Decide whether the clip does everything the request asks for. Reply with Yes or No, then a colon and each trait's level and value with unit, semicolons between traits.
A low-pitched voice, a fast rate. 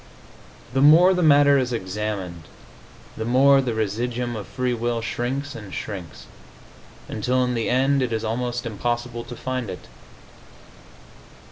No: low, 120 Hz; average, 140 wpm